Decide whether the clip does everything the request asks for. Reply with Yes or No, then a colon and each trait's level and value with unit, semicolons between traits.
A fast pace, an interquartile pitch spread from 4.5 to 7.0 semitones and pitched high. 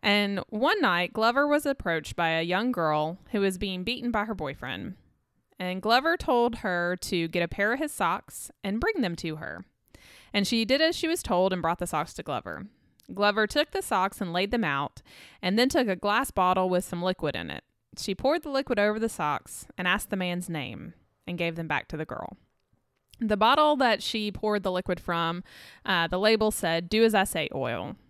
Yes: fast, 215 wpm; average, 4.9 semitones; high, 200 Hz